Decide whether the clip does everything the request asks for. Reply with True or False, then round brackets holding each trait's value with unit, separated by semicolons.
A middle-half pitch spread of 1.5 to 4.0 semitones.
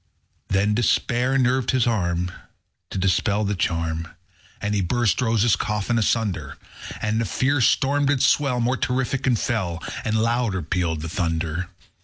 False (5.3 semitones)